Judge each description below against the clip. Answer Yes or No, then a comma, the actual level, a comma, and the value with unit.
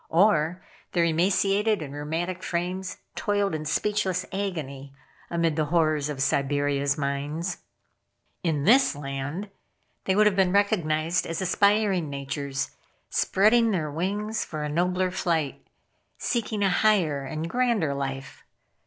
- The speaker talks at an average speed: No, slow, 125 wpm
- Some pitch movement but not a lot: Yes, average, 5.0 semitones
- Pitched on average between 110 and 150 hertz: No, medium, 170 Hz